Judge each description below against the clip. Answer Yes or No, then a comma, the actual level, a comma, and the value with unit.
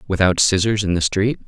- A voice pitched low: Yes, low, 100 Hz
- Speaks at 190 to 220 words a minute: Yes, fast, 205 wpm